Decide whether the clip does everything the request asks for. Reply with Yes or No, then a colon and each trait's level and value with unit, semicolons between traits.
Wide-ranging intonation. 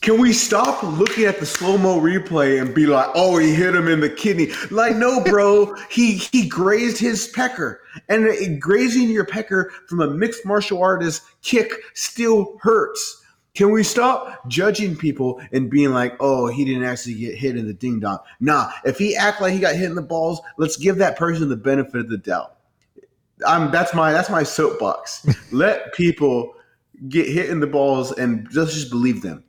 Yes: wide, 6.7 semitones